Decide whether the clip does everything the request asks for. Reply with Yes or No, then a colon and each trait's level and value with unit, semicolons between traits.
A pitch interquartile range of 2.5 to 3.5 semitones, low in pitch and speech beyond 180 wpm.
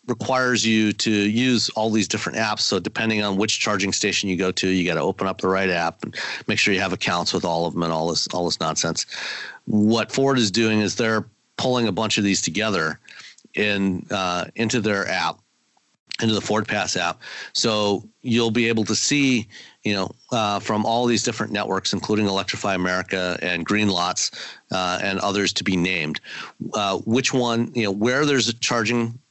Yes: average, 3.1 semitones; low, 105 Hz; average, 200 wpm